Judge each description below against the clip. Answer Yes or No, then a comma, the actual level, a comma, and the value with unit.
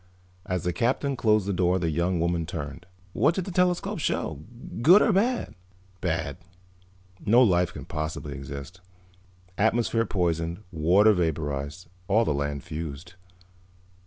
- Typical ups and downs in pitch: No, wide, 5.9 semitones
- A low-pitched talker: Yes, very low, 90 Hz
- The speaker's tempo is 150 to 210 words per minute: No, slow, 135 wpm